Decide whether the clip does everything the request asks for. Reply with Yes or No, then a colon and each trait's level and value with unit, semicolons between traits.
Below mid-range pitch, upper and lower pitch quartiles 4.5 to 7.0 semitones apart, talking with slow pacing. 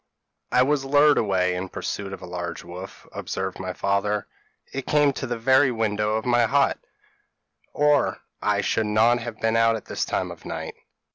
No: low, 110 Hz; average, 5.0 semitones; average, 195 wpm